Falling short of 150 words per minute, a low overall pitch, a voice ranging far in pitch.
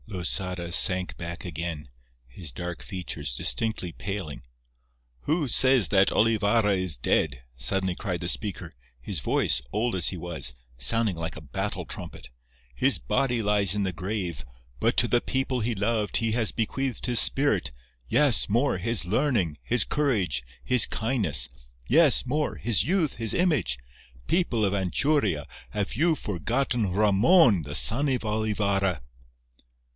Yes: slow, 135 wpm; low, 100 Hz; wide, 6.0 semitones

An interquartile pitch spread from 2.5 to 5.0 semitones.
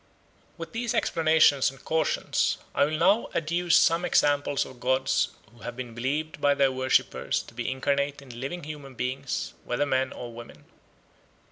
Yes: average, 3.3 semitones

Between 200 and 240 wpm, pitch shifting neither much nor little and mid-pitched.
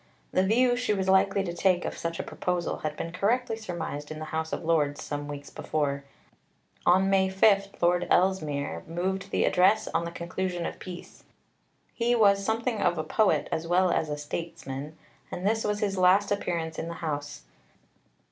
No: average, 185 wpm; average, 3.7 semitones; medium, 180 Hz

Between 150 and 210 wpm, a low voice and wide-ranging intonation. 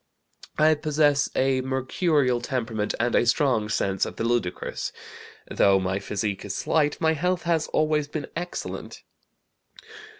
No: slow, 135 wpm; low, 130 Hz; wide, 5.8 semitones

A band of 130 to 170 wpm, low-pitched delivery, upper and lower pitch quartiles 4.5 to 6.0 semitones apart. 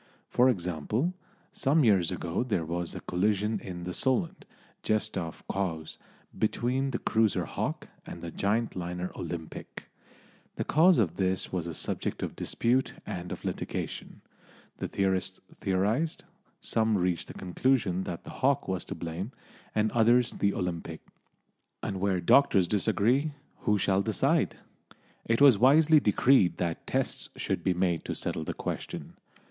Yes: average, 150 wpm; low, 100 Hz; average, 5.3 semitones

